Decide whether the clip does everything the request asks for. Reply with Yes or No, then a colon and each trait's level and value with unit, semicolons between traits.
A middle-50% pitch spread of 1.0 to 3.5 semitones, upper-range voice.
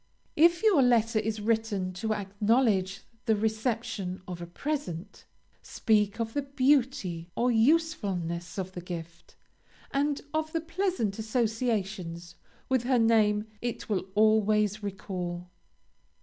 No: average, 4.8 semitones; high, 215 Hz